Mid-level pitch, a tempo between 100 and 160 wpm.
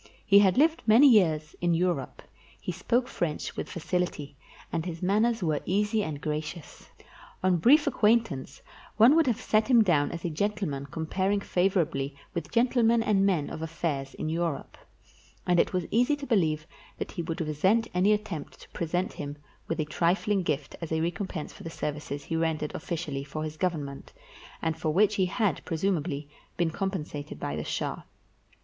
No: medium, 175 Hz; average, 175 wpm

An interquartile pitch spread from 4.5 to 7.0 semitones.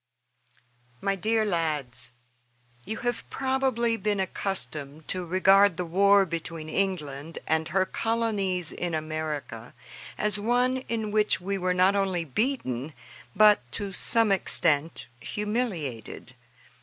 Yes: average, 5.0 semitones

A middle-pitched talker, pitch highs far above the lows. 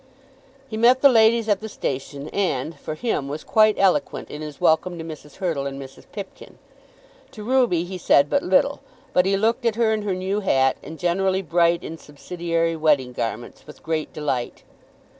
Yes: medium, 175 Hz; wide, 5.8 semitones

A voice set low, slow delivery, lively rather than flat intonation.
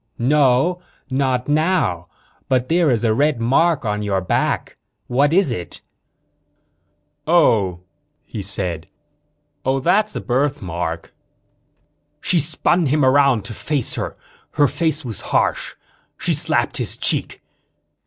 Yes: low, 130 Hz; slow, 125 wpm; wide, 6.2 semitones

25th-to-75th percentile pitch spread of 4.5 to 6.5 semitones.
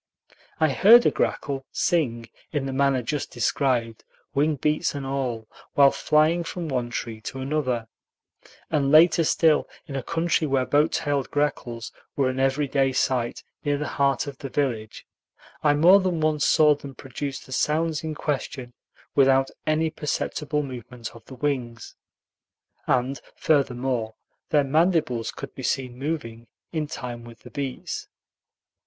No: average, 3.2 semitones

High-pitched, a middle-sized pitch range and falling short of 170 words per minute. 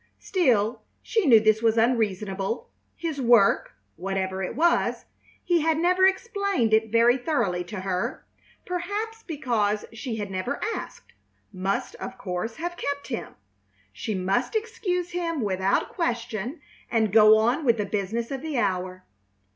No: high, 230 Hz; wide, 8.2 semitones; average, 145 wpm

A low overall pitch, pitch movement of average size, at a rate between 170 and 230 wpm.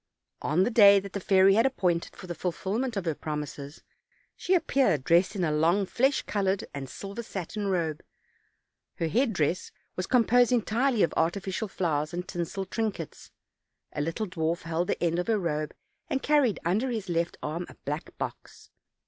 No: medium, 185 Hz; average, 4.6 semitones; average, 175 wpm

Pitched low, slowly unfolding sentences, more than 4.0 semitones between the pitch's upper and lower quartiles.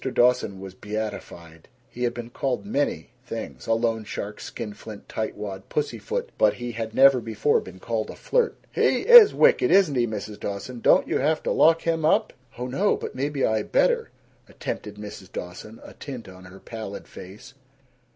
No: low, 115 Hz; average, 170 wpm; average, 4.9 semitones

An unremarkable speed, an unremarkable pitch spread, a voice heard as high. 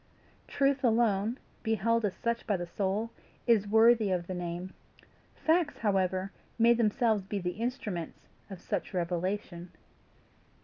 No: slow, 130 wpm; average, 3.9 semitones; high, 205 Hz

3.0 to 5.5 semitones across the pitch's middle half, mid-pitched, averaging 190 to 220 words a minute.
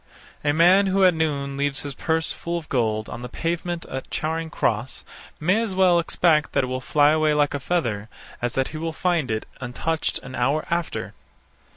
Yes: average, 4.3 semitones; medium, 155 Hz; average, 200 wpm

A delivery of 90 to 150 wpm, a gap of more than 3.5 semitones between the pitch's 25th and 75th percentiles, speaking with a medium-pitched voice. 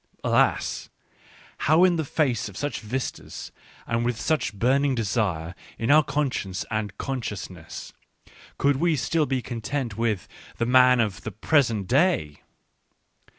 No: slow, 135 wpm; average, 5.0 semitones; low, 125 Hz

